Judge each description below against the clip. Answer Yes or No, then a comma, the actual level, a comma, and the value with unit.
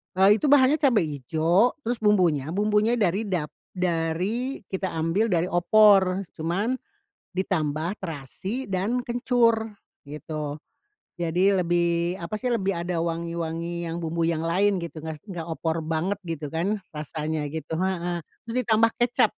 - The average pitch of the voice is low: No, medium, 175 Hz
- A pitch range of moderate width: Yes, average, 4.2 semitones